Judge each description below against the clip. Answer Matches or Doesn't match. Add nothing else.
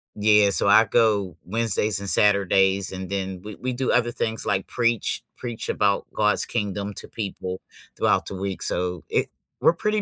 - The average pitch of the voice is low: Matches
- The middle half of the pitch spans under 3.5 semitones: Matches